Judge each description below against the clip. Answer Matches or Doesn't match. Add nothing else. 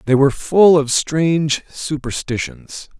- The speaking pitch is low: Doesn't match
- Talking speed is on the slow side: Matches